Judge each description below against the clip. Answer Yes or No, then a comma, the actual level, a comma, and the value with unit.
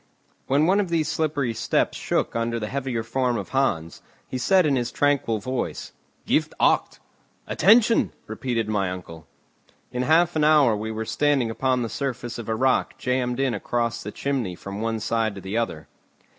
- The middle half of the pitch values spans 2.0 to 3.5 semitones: No, average, 3.9 semitones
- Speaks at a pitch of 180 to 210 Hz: No, low, 120 Hz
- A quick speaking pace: No, average, 180 wpm